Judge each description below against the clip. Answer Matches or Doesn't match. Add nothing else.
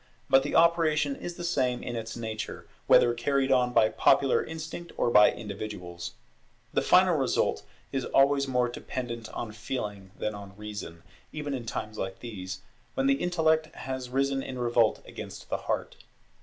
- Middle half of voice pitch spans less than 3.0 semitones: Doesn't match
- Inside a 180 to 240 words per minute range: Doesn't match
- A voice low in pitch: Matches